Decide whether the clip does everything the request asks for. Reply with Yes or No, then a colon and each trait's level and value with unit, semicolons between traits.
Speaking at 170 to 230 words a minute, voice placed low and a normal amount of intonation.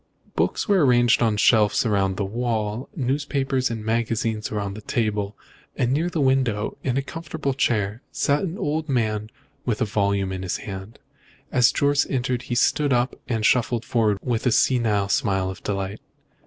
Yes: average, 175 wpm; low, 115 Hz; average, 4.0 semitones